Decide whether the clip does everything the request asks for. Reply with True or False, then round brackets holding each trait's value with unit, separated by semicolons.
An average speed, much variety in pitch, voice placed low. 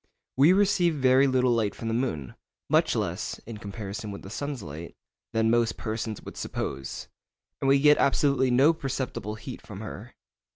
False (170 wpm; 4.4 semitones; 120 Hz)